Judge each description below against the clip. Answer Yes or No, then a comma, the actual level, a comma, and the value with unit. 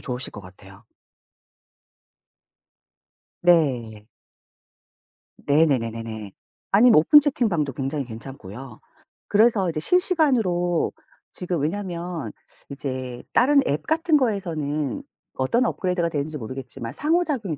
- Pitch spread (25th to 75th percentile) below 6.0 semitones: No, wide, 8.2 semitones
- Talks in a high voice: No, medium, 155 Hz